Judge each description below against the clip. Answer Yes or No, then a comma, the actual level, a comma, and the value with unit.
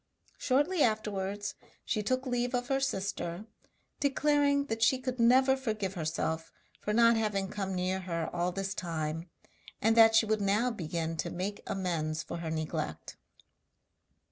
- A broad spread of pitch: Yes, wide, 5.7 semitones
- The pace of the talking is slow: No, average, 150 wpm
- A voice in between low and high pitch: No, high, 205 Hz